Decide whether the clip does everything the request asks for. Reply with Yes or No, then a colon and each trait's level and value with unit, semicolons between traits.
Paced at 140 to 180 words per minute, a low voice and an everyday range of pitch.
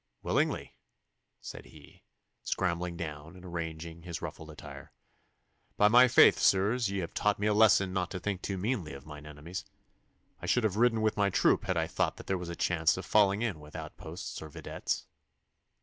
No: average, 190 wpm; very low, 90 Hz; average, 4.0 semitones